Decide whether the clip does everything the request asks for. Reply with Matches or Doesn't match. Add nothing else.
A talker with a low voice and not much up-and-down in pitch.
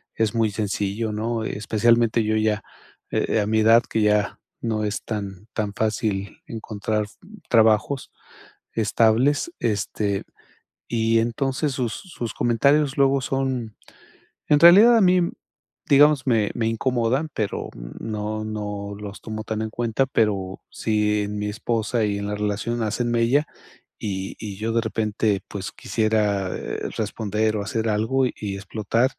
Matches